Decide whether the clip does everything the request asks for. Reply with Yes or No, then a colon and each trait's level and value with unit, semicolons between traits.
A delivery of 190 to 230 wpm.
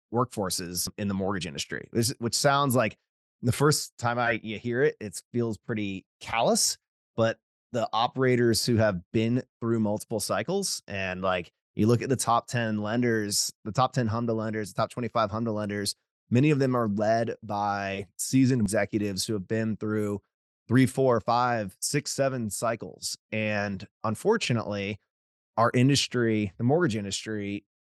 No: average, 160 wpm